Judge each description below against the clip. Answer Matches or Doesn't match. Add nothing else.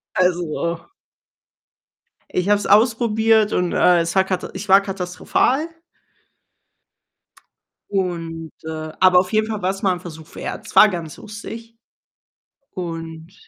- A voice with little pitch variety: Doesn't match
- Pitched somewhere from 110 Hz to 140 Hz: Doesn't match